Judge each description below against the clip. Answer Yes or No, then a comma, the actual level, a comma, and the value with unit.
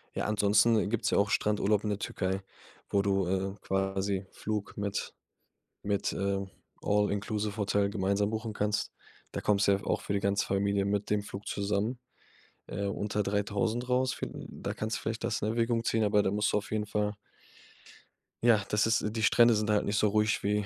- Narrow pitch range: Yes, narrow, 1.3 semitones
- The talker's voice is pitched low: Yes, low, 105 Hz